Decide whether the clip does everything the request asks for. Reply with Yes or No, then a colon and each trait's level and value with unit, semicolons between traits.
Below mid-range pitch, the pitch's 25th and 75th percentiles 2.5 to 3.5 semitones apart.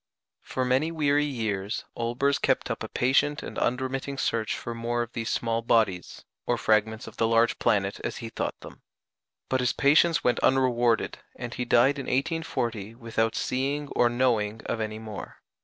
Yes: low, 120 Hz; average, 2.9 semitones